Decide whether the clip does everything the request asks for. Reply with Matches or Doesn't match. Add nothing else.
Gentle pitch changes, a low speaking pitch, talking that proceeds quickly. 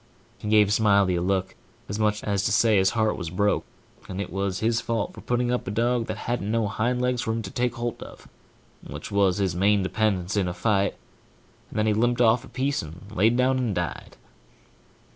Doesn't match